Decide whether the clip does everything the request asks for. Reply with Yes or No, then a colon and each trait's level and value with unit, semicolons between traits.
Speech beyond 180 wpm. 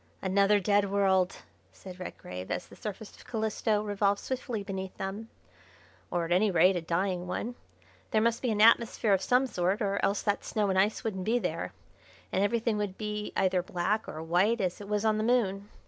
Yes: average, 195 wpm